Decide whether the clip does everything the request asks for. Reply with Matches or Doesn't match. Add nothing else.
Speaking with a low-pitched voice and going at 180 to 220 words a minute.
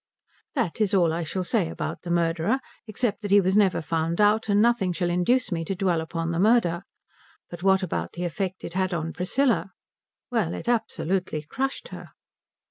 Doesn't match